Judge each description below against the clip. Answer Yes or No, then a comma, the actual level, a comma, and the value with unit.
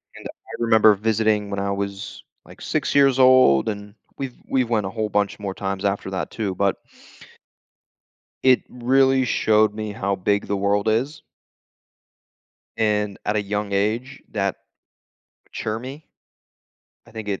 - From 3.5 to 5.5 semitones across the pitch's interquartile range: No, average, 2.7 semitones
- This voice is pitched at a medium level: No, low, 105 Hz